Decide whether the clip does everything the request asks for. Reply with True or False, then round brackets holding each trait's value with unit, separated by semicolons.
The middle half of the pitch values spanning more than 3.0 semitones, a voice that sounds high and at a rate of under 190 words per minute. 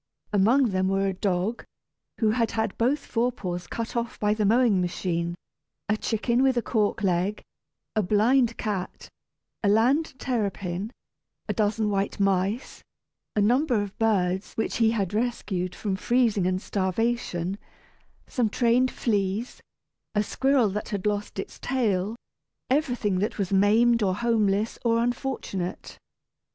True (3.4 semitones; 210 Hz; 140 wpm)